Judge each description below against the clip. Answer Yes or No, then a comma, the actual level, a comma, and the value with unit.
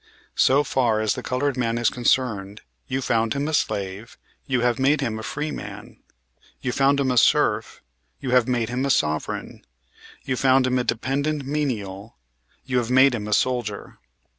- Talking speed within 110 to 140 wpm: No, average, 180 wpm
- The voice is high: No, low, 125 Hz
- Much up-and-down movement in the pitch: No, average, 3.2 semitones